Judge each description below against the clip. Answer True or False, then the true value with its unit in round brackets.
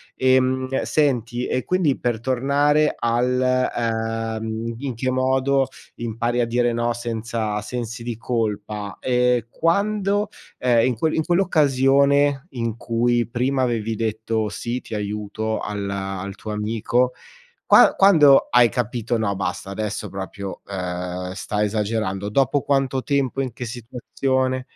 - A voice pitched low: True (120 Hz)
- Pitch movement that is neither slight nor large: True (3.1 semitones)